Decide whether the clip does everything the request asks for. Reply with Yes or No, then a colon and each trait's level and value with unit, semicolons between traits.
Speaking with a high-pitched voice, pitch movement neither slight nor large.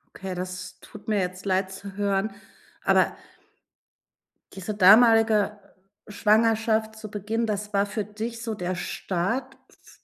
No: high, 210 Hz; narrow, 2.3 semitones